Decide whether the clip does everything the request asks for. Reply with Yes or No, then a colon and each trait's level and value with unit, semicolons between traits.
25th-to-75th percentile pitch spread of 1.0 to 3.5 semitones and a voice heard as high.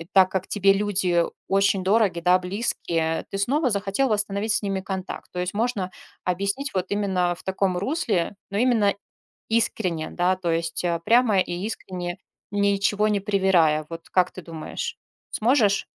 Yes: narrow, 2.6 semitones; high, 195 Hz